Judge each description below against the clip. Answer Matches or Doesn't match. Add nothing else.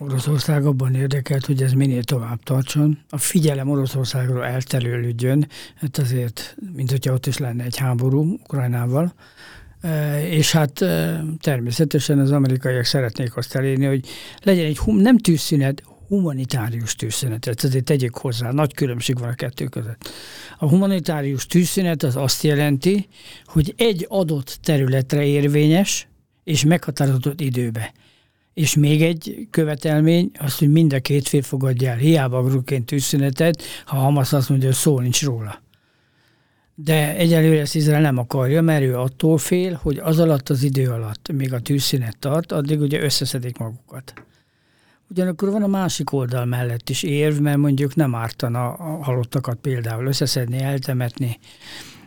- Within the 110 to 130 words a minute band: Doesn't match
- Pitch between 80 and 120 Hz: Doesn't match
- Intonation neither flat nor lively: Matches